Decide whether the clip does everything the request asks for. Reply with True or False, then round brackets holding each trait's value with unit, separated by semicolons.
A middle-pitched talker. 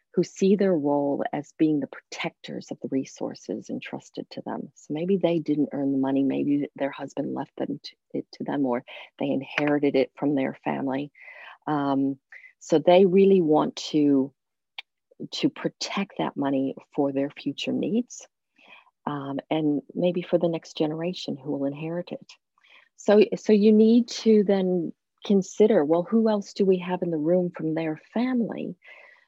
True (165 Hz)